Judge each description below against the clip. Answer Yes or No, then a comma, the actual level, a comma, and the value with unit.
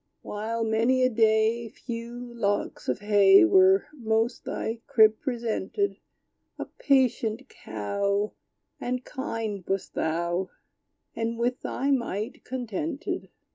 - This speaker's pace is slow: Yes, slow, 110 wpm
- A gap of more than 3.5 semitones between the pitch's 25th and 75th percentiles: No, average, 3.2 semitones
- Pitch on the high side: Yes, high, 230 Hz